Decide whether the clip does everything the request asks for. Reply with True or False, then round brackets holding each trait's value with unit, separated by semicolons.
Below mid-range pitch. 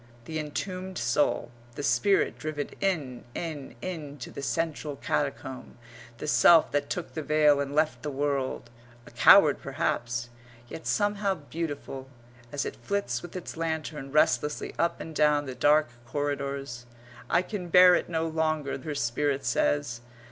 False (150 Hz)